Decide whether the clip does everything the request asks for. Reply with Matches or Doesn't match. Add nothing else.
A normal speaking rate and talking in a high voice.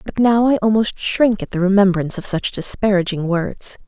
Matches